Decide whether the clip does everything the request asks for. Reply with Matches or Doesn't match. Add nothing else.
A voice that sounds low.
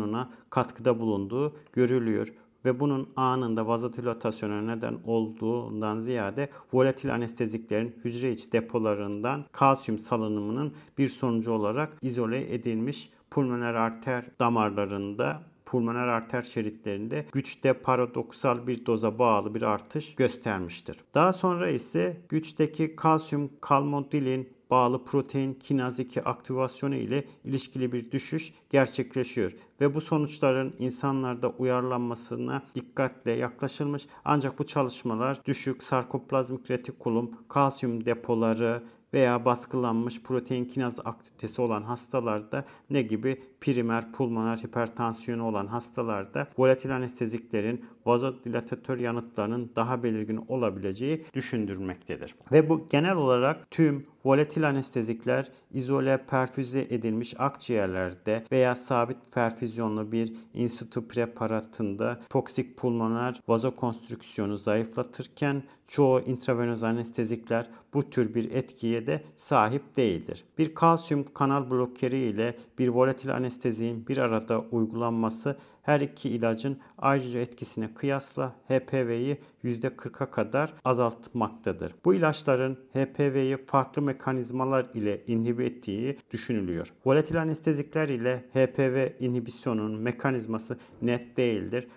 Matches